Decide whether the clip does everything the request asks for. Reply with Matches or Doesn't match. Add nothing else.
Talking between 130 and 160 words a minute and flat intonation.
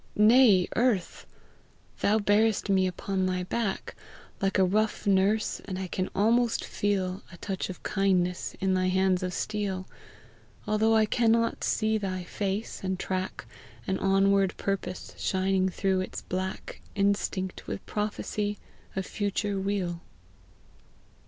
Matches